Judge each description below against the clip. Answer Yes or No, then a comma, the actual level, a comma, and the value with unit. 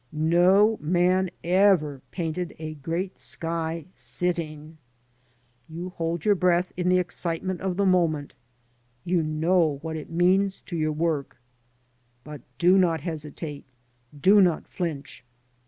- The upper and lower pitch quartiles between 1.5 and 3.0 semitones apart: Yes, average, 2.7 semitones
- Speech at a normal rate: No, slow, 125 wpm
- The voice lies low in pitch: No, medium, 170 Hz